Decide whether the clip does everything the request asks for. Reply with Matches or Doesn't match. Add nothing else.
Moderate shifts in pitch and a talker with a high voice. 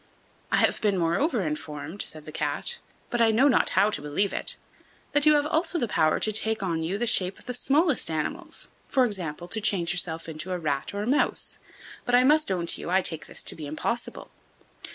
Doesn't match